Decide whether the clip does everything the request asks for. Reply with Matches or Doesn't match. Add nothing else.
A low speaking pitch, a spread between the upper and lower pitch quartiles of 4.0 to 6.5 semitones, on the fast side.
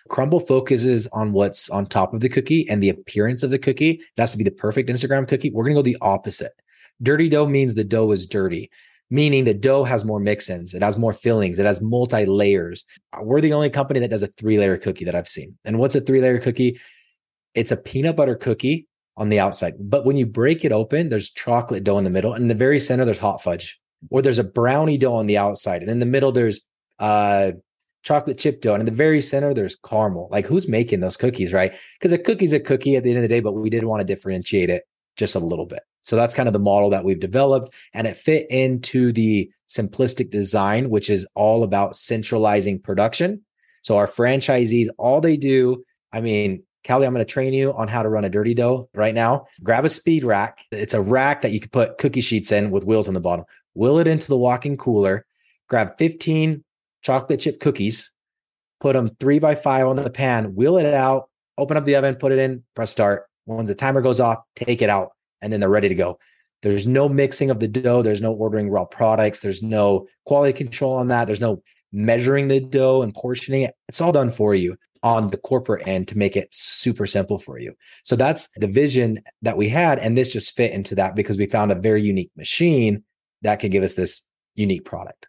Matches